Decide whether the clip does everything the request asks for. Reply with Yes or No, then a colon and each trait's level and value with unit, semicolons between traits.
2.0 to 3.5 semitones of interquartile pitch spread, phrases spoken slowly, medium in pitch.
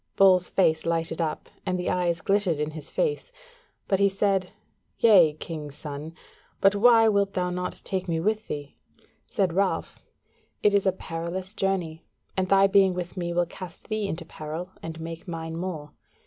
No: average, 3.2 semitones; average, 175 wpm; medium, 180 Hz